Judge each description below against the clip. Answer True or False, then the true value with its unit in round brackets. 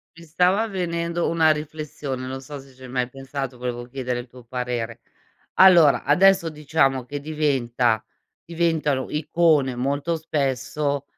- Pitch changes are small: False (4.0 semitones)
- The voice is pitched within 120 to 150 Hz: True (140 Hz)